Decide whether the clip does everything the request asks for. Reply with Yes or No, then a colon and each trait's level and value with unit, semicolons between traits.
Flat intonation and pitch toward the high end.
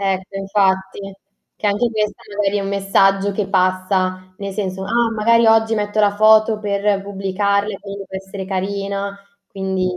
Yes: narrow, 1.4 semitones; high, 200 Hz